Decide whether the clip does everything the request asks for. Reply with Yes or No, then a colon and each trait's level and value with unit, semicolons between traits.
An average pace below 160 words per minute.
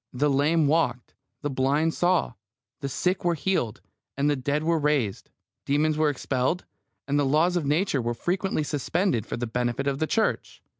No: average, 170 wpm